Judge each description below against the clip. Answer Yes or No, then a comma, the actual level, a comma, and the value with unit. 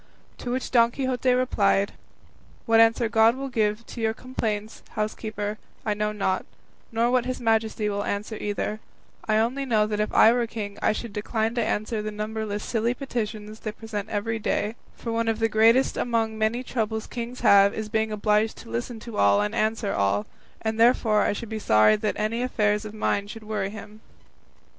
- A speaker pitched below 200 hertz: No, high, 220 Hz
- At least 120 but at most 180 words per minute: No, average, 195 wpm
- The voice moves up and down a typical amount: No, narrow, 1.7 semitones